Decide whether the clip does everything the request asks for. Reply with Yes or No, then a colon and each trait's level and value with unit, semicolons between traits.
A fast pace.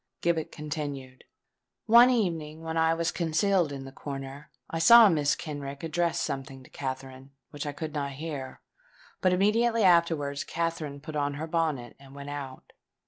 No: average, 160 wpm